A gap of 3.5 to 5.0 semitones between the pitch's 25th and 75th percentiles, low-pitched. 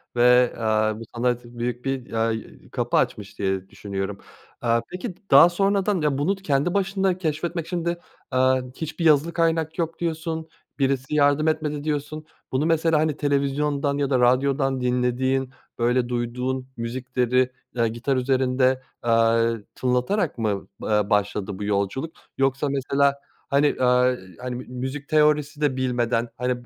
Yes: average, 3.8 semitones; low, 130 Hz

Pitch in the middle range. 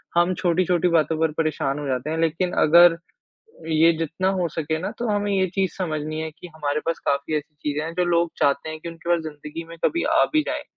Yes: medium, 165 Hz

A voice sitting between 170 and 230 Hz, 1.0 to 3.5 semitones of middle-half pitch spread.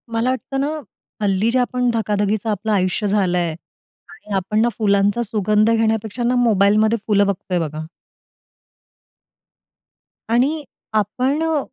Yes: high, 215 Hz; average, 3.1 semitones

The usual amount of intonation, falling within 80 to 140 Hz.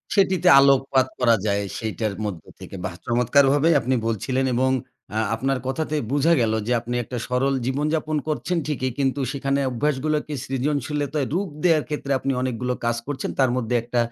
Yes: average, 3.3 semitones; low, 135 Hz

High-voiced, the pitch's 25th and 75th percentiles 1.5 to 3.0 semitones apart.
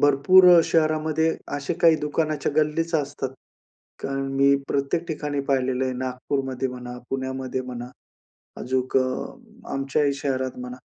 No: medium, 140 Hz; average, 2.7 semitones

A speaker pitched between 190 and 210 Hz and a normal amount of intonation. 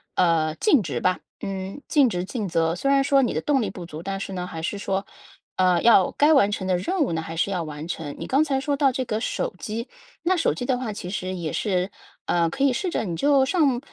No: high, 200 Hz; wide, 7.3 semitones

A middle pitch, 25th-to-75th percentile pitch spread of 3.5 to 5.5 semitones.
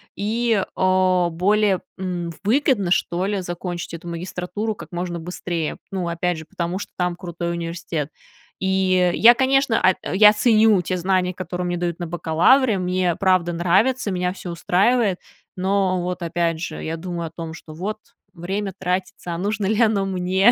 No: medium, 180 Hz; narrow, 2.4 semitones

